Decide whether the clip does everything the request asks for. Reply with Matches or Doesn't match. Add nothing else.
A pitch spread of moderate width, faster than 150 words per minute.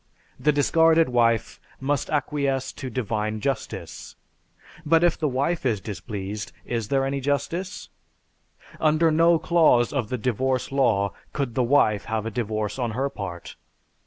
Doesn't match